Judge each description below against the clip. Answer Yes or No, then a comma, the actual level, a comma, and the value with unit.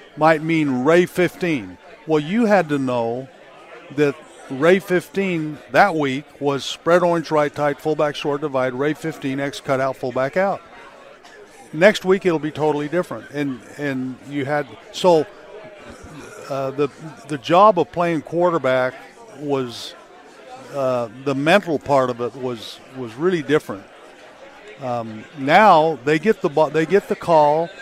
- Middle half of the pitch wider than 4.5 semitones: No, average, 4.2 semitones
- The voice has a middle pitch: Yes, medium, 150 Hz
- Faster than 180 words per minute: No, average, 145 wpm